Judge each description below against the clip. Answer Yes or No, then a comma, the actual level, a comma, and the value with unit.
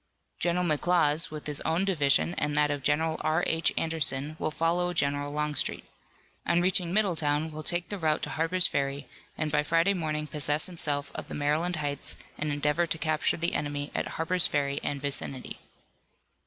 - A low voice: No, medium, 155 Hz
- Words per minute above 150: Yes, average, 175 wpm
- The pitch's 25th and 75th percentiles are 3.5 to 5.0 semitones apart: No, narrow, 2.6 semitones